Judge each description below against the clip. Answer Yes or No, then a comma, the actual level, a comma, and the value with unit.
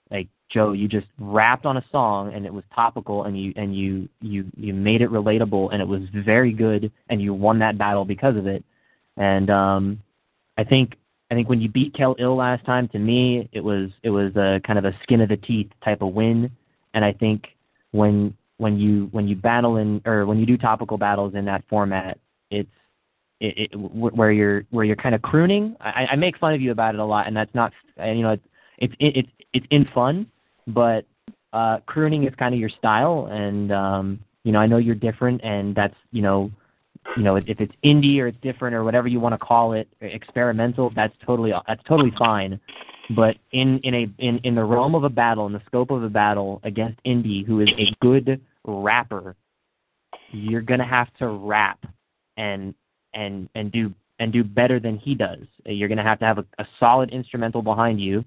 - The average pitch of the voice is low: Yes, low, 110 Hz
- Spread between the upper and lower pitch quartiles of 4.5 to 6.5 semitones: No, average, 3.0 semitones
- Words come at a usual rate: No, fast, 215 wpm